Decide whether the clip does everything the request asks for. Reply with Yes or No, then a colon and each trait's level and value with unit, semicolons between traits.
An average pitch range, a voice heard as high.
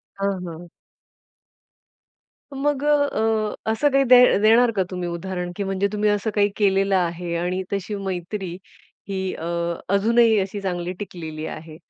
Yes: average, 3.5 semitones; high, 195 Hz